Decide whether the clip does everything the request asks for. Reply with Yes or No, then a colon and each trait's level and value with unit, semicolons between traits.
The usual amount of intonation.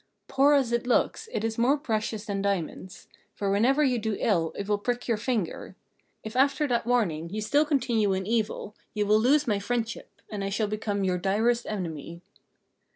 Yes: average, 3.4 semitones